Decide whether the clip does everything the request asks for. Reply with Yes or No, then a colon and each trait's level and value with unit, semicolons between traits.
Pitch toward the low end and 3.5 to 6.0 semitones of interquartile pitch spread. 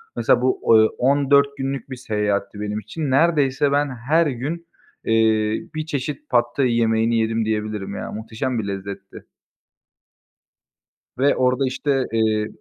Yes: low, 120 Hz; average, 4.4 semitones